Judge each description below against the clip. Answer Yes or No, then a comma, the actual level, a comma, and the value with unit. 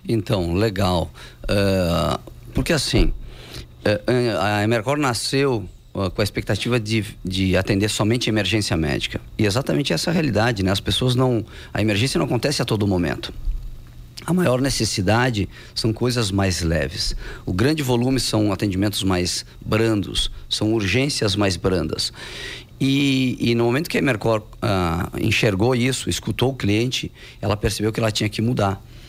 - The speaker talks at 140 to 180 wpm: Yes, average, 155 wpm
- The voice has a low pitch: Yes, low, 110 Hz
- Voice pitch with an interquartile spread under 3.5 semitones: No, average, 4.1 semitones